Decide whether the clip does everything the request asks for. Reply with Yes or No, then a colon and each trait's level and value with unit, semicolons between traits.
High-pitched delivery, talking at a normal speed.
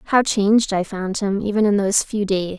No: high, 205 Hz; fast, 230 wpm